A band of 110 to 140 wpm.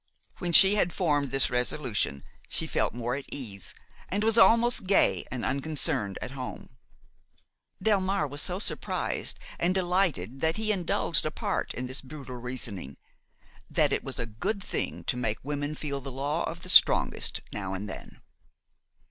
No: average, 160 wpm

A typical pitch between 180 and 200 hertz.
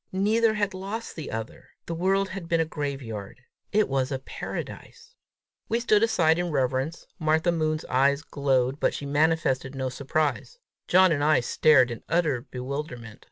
No: medium, 155 Hz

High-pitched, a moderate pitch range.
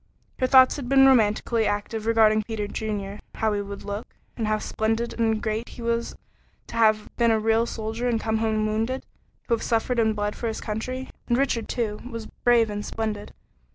No: high, 225 Hz; narrow, 1.6 semitones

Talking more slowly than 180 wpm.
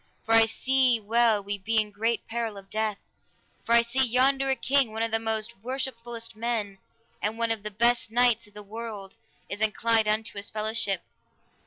No: average, 190 wpm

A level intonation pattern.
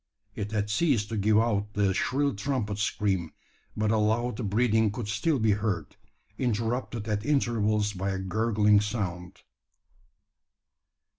Yes: narrow, 2.2 semitones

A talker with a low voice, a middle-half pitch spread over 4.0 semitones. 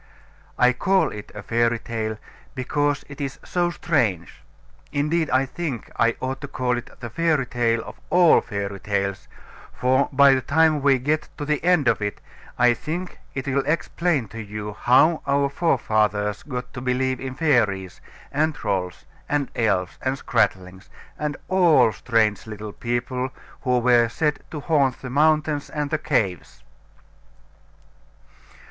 Yes: low, 130 Hz; average, 4.9 semitones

